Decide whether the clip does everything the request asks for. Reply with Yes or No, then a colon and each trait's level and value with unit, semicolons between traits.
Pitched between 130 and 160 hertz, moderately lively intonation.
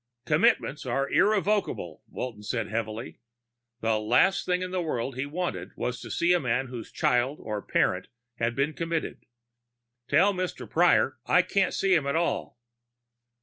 No: medium, 140 Hz; wide, 7.6 semitones